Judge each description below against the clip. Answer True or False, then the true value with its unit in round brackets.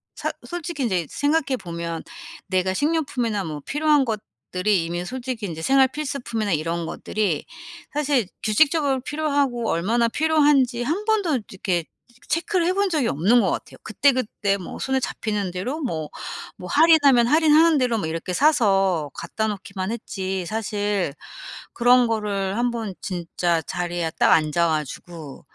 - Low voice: False (225 Hz)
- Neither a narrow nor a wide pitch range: False (7.6 semitones)